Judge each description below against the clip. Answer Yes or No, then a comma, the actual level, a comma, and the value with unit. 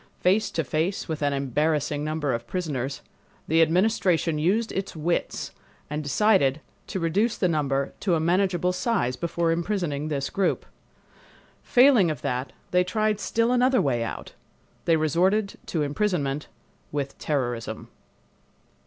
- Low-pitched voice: No, medium, 165 Hz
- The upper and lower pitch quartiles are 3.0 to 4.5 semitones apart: No, average, 5.0 semitones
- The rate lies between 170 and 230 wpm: No, slow, 135 wpm